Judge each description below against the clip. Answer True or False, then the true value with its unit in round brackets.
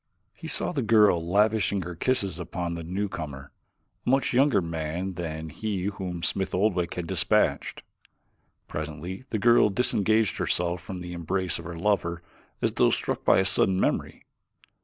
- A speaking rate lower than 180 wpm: True (160 wpm)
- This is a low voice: True (90 Hz)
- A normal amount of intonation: True (3.4 semitones)